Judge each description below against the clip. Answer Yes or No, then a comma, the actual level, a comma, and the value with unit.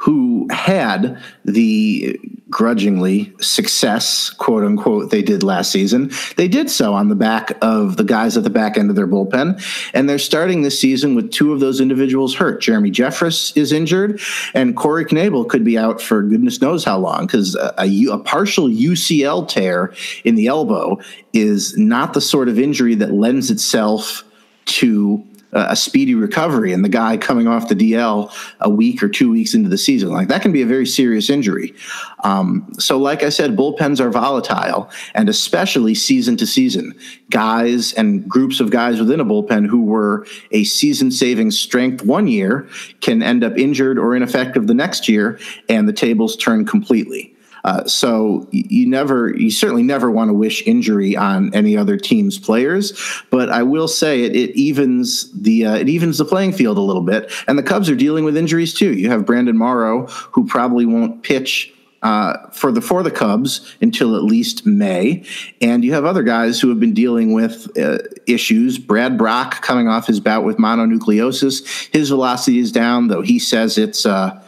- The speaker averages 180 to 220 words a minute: Yes, average, 185 wpm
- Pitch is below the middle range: No, high, 200 Hz